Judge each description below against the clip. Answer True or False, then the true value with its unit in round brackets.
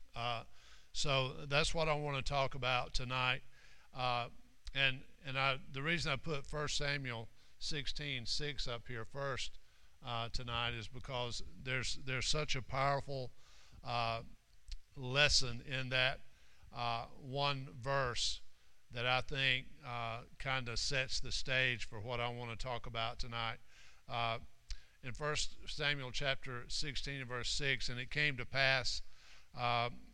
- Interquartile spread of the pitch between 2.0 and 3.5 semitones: True (2.7 semitones)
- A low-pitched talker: True (130 Hz)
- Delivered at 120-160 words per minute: True (140 wpm)